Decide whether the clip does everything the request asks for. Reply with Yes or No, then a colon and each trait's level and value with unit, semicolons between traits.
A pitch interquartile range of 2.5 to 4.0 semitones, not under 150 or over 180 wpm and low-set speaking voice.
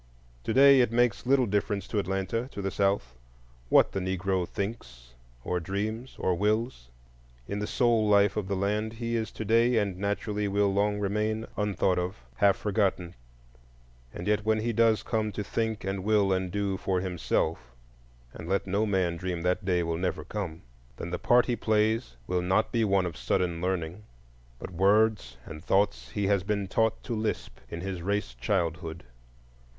Yes: average, 3.3 semitones; average, 175 wpm; low, 100 Hz